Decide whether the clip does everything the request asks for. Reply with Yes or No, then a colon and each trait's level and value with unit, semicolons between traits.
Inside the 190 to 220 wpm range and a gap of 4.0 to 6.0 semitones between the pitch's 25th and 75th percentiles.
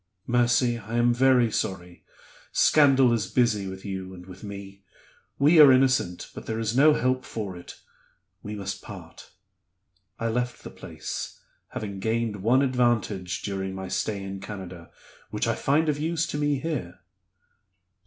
No: average, 155 wpm; average, 4.9 semitones